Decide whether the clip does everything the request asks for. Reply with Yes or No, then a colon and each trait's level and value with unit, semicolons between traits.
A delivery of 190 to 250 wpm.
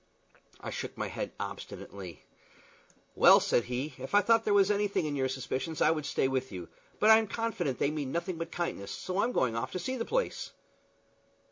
Yes: average, 200 wpm